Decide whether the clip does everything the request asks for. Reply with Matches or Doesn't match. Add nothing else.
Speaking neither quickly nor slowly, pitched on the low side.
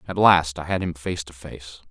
Doesn't match